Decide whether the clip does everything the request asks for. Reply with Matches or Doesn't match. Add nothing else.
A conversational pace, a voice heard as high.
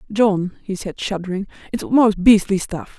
Matches